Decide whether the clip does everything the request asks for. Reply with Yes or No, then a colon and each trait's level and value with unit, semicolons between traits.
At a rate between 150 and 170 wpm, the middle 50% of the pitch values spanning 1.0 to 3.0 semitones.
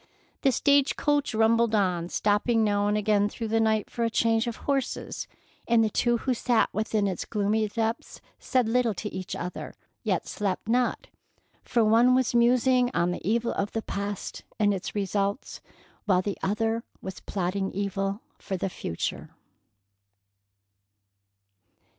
Yes: average, 155 wpm; average, 2.7 semitones